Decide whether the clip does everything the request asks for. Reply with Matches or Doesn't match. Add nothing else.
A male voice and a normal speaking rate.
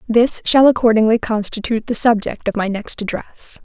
Doesn't match